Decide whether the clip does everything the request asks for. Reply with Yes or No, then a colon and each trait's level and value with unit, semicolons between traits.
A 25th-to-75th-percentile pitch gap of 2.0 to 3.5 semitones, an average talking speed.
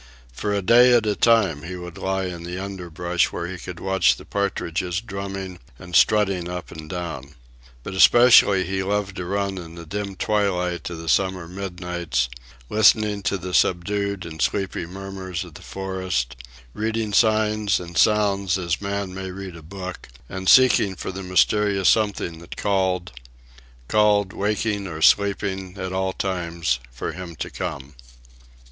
Yes: narrow, 2.4 semitones; average, 160 wpm